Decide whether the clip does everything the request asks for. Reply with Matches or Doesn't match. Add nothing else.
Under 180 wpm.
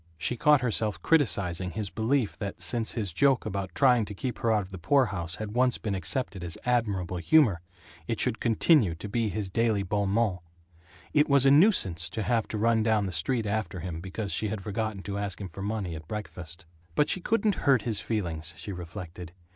Doesn't match